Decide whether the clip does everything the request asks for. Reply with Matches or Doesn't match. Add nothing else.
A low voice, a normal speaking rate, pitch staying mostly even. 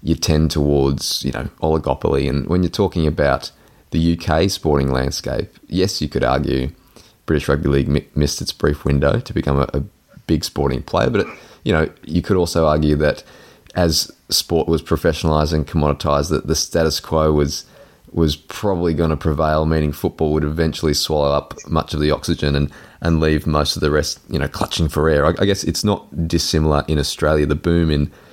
Matches